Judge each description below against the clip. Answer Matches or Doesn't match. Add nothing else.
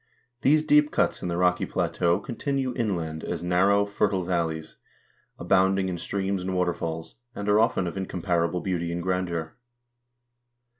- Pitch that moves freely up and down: Doesn't match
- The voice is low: Matches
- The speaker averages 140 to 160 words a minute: Matches